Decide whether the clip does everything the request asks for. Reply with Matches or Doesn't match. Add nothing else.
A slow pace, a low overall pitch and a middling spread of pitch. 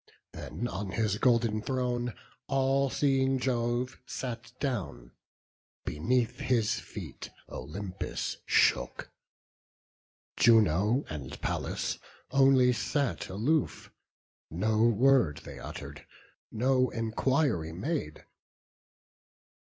Matches